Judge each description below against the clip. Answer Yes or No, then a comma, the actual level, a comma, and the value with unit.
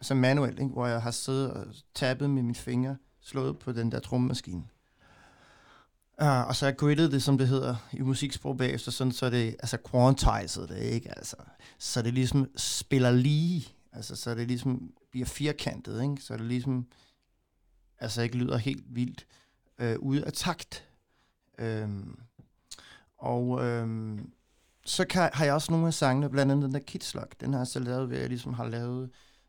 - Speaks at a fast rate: No, average, 180 wpm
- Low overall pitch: Yes, low, 125 Hz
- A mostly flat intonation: Yes, narrow, 2.2 semitones